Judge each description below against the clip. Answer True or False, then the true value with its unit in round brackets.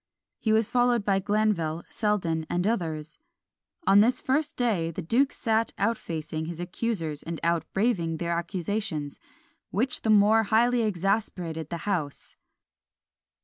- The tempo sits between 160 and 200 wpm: False (140 wpm)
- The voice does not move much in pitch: False (5.2 semitones)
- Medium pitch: False (195 Hz)